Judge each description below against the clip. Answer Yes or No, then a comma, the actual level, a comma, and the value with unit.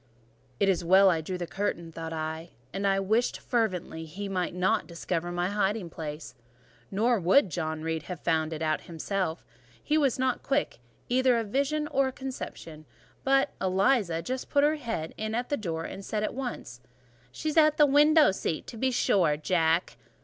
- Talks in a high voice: Yes, high, 195 Hz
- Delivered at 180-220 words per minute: Yes, average, 185 wpm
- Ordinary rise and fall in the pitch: No, wide, 7.4 semitones